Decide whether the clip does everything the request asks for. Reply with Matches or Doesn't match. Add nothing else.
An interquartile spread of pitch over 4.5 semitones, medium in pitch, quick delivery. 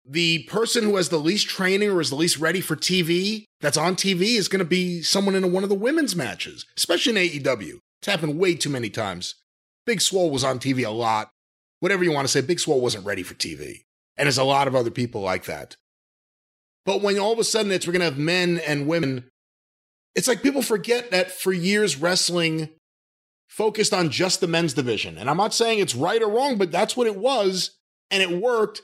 Matches